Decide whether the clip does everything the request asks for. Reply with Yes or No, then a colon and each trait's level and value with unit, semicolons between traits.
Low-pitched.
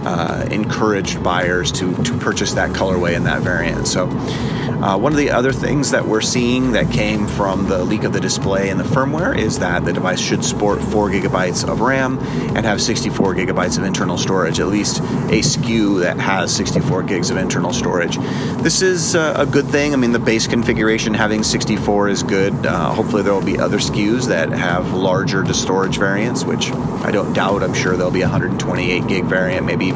Yes: low, 115 Hz